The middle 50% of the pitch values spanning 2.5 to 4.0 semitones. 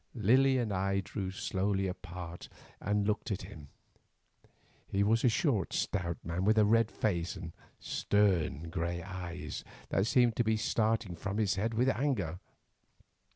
Yes: average, 3.7 semitones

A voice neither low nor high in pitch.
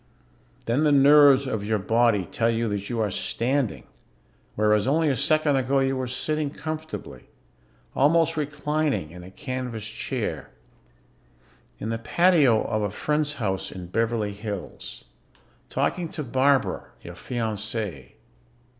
No: low, 125 Hz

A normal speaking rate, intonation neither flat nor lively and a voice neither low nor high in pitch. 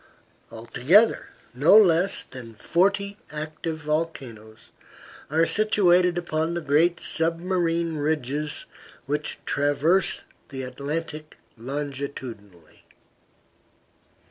No: slow, 80 wpm; average, 3.7 semitones; medium, 155 Hz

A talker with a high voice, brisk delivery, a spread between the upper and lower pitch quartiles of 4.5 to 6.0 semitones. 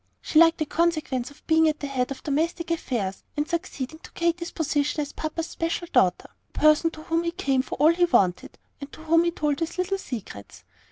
No: very high, 310 Hz; fast, 215 wpm; average, 3.2 semitones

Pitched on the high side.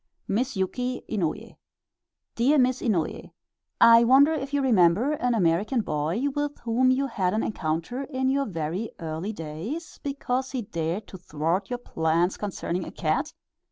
Yes: high, 225 Hz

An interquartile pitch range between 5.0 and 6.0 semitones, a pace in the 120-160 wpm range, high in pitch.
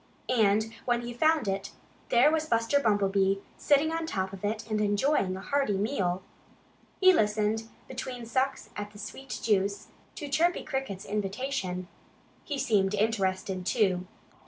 Yes: average, 5.3 semitones; average, 145 wpm; high, 215 Hz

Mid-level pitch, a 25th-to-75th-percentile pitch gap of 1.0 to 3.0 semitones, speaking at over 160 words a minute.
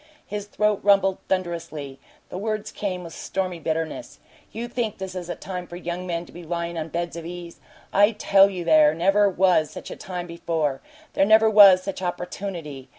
Yes: medium, 180 Hz; average, 2.7 semitones; average, 190 wpm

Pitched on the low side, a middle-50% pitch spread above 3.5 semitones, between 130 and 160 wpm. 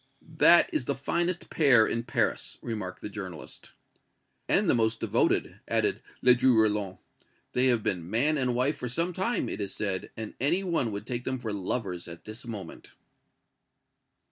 No: low, 115 Hz; average, 4.2 semitones; average, 170 wpm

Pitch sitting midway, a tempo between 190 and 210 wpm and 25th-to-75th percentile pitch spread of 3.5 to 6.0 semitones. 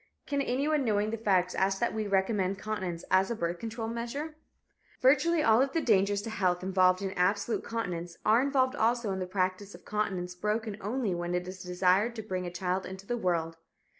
No: high, 200 Hz; average, 200 wpm; average, 4.0 semitones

